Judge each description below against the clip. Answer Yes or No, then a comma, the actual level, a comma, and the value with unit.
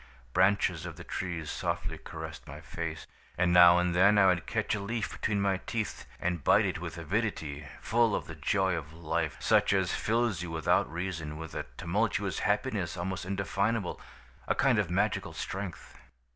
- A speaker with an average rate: Yes, average, 175 wpm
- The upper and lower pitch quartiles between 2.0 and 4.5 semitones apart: Yes, average, 3.5 semitones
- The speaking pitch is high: No, very low, 90 Hz